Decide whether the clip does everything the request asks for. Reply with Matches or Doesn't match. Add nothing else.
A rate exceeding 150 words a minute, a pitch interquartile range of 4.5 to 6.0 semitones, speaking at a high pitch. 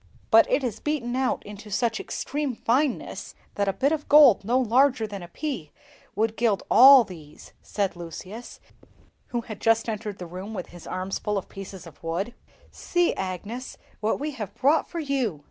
Matches